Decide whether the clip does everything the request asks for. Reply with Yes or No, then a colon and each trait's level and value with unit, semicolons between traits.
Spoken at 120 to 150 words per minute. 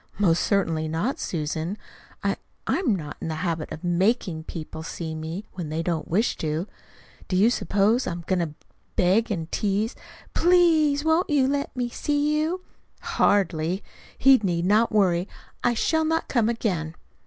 No: average, 165 wpm